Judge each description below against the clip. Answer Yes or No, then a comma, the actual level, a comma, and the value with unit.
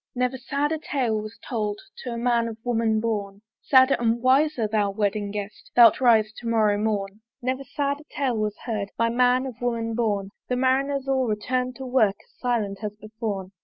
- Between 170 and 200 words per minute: Yes, average, 190 wpm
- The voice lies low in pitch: No, high, 230 Hz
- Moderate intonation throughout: Yes, average, 3.3 semitones